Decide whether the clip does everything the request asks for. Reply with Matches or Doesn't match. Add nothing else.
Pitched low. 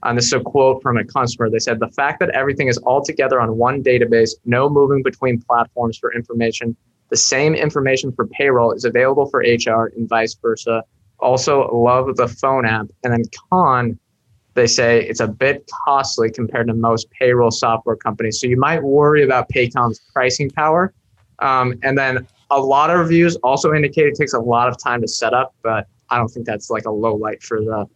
Matches